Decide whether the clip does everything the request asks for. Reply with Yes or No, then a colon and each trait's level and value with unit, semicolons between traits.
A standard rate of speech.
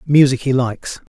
Yes: average, 155 wpm